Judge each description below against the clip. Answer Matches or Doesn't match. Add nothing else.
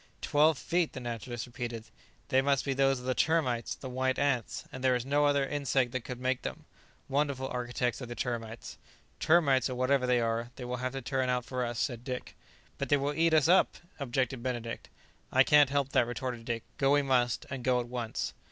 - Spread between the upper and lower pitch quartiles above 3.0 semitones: Doesn't match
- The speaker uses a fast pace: Matches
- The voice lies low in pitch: Matches